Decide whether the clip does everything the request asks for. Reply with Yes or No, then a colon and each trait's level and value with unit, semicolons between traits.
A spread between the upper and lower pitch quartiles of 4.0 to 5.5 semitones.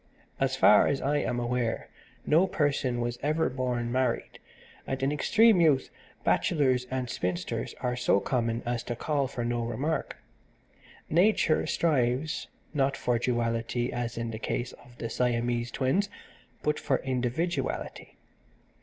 No: average, 3.4 semitones